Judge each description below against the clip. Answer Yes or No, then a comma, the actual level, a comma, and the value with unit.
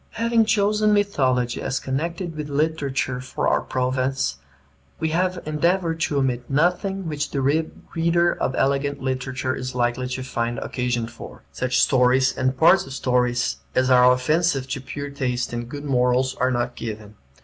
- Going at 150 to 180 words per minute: Yes, average, 160 wpm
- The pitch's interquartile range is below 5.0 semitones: Yes, average, 4.1 semitones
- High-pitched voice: No, low, 135 Hz